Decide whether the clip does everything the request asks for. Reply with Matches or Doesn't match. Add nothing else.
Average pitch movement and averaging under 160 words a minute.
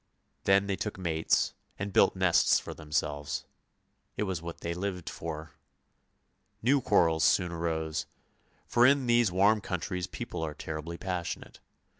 Matches